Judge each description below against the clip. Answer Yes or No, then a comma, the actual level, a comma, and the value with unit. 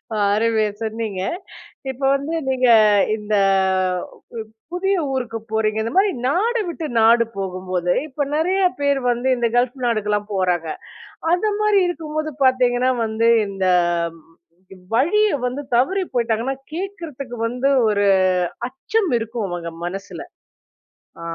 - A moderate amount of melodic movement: No, wide, 6.1 semitones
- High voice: Yes, high, 245 Hz